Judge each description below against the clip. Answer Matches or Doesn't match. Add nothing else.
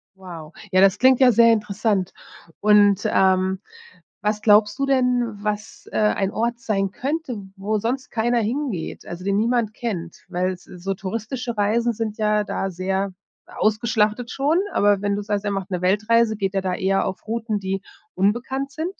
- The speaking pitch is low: Doesn't match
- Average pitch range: Matches